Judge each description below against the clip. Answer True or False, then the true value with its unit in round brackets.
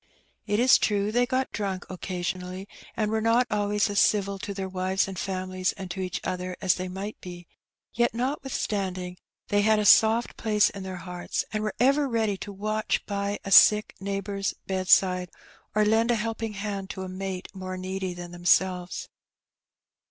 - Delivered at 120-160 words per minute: False (180 wpm)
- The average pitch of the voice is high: True (195 Hz)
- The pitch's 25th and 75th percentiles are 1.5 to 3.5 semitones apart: True (2.5 semitones)